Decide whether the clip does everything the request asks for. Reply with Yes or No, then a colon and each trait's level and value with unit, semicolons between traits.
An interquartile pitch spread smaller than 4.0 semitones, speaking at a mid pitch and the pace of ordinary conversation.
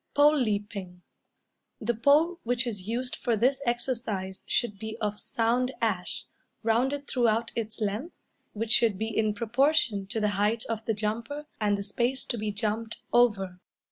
No: average, 2.8 semitones; high, 225 Hz; average, 160 wpm